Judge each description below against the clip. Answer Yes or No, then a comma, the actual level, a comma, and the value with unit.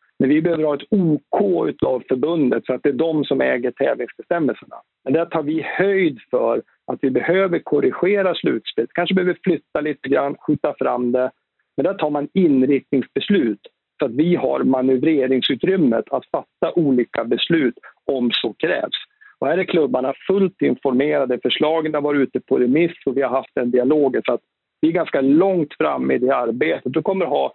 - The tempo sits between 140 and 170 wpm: No, average, 180 wpm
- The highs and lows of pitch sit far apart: No, average, 4.5 semitones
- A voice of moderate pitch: Yes, medium, 150 Hz